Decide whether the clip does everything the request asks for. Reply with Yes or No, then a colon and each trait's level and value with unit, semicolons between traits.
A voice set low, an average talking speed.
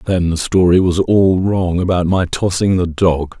Yes: very low, 90 Hz; average, 195 wpm